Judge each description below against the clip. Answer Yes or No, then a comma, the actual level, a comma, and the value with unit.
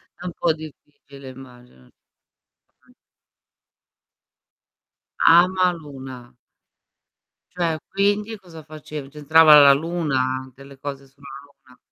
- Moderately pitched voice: Yes, medium, 145 Hz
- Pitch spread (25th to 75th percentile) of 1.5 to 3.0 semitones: No, average, 3.7 semitones